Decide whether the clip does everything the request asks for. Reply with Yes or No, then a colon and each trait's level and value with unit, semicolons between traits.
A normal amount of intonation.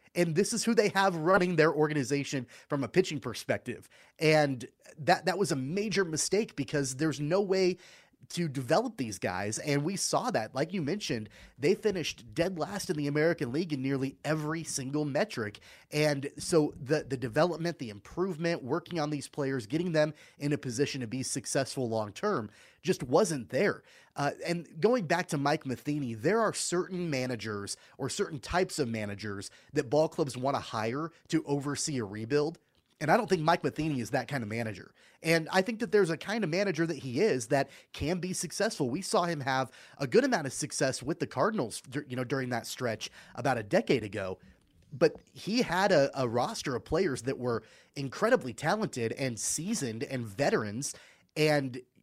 Yes: average, 4.7 semitones